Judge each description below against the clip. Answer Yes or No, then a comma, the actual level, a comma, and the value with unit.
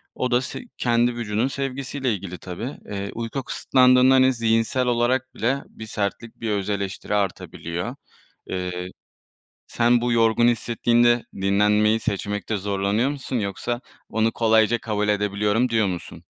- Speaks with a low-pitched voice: Yes, low, 115 Hz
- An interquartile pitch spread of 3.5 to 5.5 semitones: No, average, 3.0 semitones